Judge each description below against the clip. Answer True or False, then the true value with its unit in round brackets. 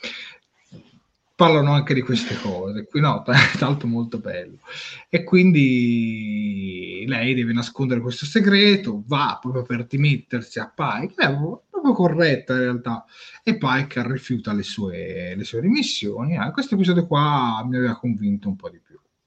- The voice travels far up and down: True (6.2 semitones)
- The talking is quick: False (160 wpm)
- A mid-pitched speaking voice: False (130 Hz)